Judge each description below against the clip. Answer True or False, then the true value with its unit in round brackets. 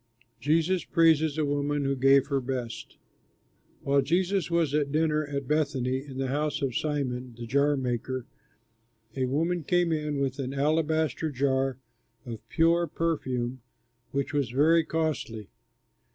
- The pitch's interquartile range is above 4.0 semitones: False (3.1 semitones)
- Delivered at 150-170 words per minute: False (140 wpm)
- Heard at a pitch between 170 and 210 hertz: False (140 Hz)